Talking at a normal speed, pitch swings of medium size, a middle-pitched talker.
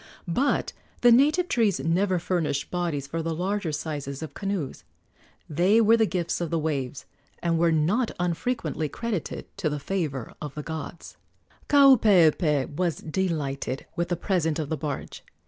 Yes: average, 155 wpm; average, 4.5 semitones; medium, 165 Hz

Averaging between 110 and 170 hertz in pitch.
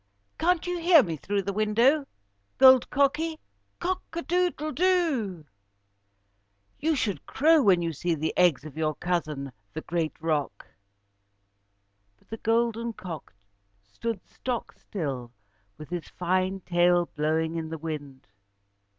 No: medium, 185 Hz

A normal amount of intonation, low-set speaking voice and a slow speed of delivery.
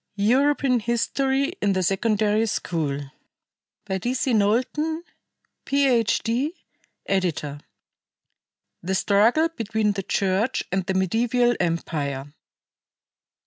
No: average, 4.9 semitones; high, 215 Hz; slow, 90 wpm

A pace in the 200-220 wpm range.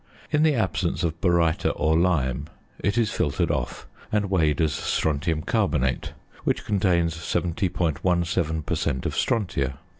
No: average, 140 wpm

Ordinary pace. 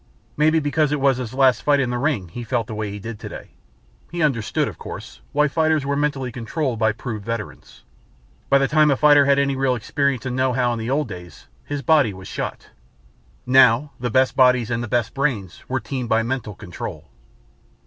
No: fast, 210 wpm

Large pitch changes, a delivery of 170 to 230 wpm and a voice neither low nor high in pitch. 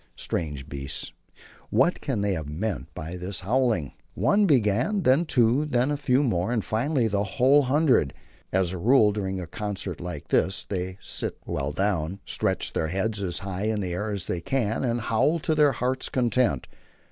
No: wide, 6.0 semitones; average, 180 wpm; low, 105 Hz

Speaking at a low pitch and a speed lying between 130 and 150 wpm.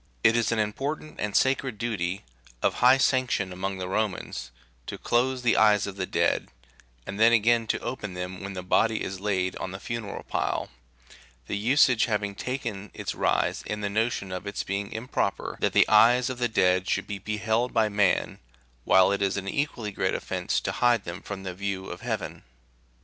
No: low, 105 Hz; average, 195 wpm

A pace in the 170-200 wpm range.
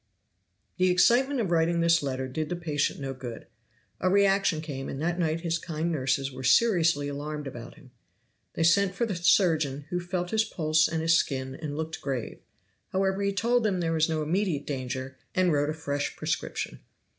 Yes: average, 190 wpm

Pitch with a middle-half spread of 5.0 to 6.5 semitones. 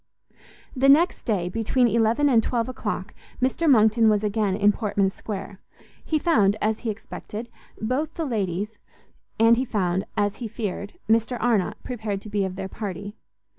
No: average, 3.0 semitones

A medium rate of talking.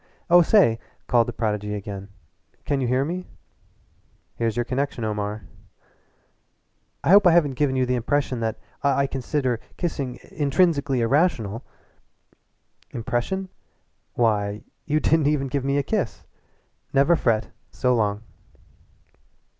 No: slow, 125 wpm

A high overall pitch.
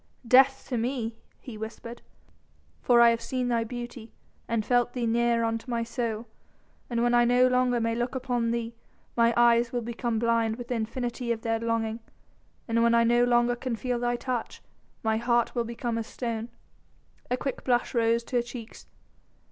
Yes: high, 235 Hz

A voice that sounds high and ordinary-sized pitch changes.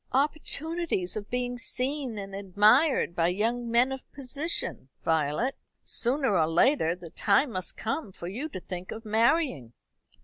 No: high, 230 Hz; wide, 6.6 semitones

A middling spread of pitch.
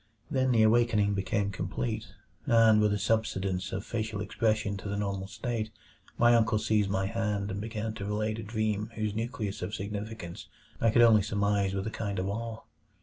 No: narrow, 1.9 semitones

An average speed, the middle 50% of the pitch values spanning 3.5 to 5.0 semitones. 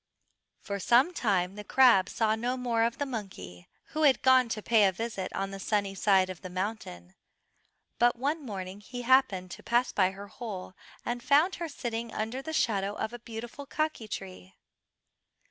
Yes: average, 180 wpm; average, 4.4 semitones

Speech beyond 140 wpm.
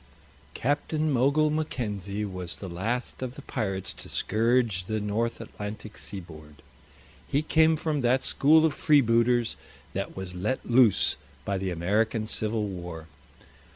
No: slow, 135 wpm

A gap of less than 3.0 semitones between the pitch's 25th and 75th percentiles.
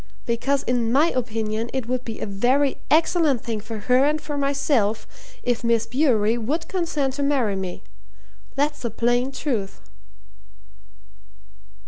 No: average, 4.1 semitones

